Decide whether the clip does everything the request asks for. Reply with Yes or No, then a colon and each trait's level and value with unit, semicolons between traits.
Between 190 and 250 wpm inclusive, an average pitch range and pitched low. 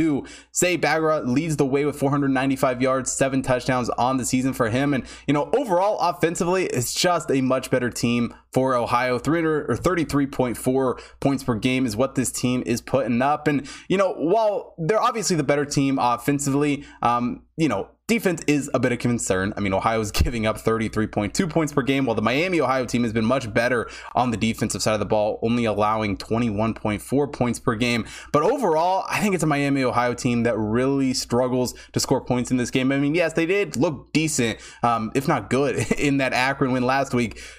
Yes: average, 200 wpm; average, 3.3 semitones; low, 130 Hz